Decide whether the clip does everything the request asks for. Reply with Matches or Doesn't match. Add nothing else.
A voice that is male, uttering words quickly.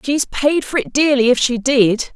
Doesn't match